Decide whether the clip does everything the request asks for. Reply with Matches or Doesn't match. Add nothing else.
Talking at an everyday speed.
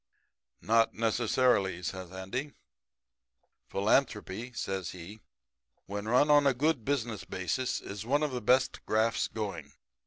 Doesn't match